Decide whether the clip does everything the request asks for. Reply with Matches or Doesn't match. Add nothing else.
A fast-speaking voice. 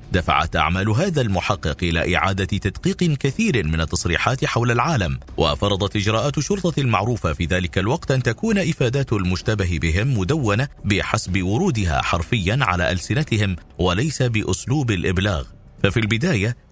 Doesn't match